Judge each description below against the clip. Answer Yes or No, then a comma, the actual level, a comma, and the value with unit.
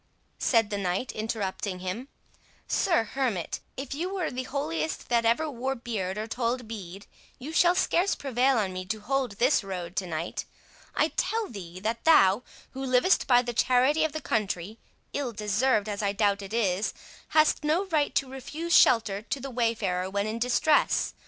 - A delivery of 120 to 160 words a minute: No, average, 170 wpm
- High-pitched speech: Yes, high, 230 Hz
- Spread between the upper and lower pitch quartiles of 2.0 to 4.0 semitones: No, average, 5.2 semitones